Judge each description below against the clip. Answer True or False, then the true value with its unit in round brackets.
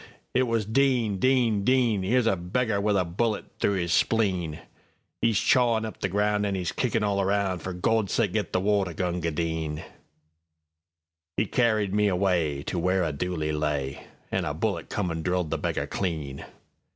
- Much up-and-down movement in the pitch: False (4.6 semitones)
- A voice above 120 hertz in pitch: False (95 Hz)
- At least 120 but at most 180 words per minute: True (155 wpm)